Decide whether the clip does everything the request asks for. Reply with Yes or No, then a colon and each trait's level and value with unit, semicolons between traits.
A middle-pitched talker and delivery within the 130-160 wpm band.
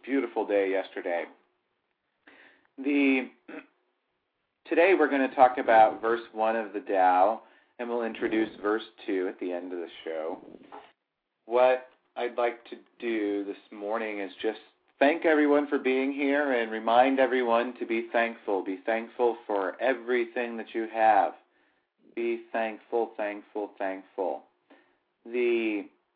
No: low, 115 Hz; slow, 135 wpm